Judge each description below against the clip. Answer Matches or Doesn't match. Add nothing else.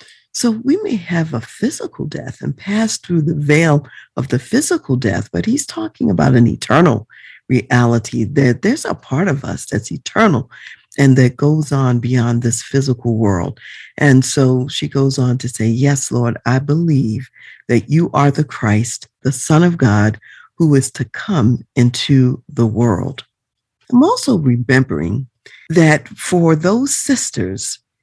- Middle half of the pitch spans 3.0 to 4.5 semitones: Doesn't match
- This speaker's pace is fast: Doesn't match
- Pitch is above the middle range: Doesn't match